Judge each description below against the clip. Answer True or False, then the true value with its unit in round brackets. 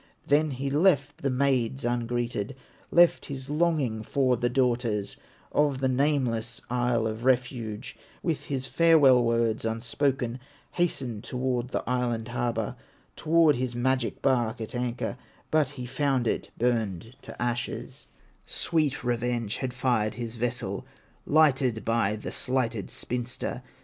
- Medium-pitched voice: False (125 Hz)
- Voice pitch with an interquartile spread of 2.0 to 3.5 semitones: True (2.7 semitones)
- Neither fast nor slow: False (130 wpm)